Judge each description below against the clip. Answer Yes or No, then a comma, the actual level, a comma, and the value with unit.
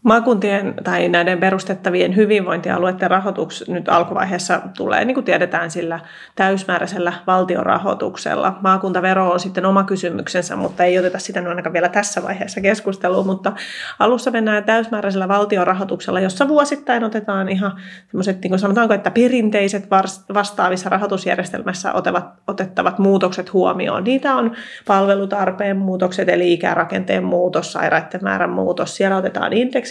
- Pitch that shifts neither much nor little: No, narrow, 1.9 semitones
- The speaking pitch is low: No, high, 195 Hz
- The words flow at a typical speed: Yes, average, 125 wpm